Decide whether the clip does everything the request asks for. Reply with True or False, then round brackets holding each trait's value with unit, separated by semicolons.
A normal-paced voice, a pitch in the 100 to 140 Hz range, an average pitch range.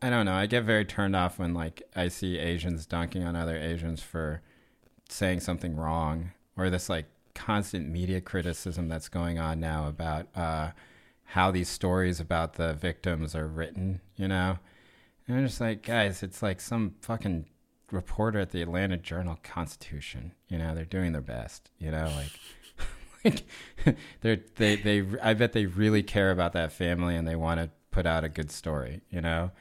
False (180 wpm; 90 Hz; 3.0 semitones)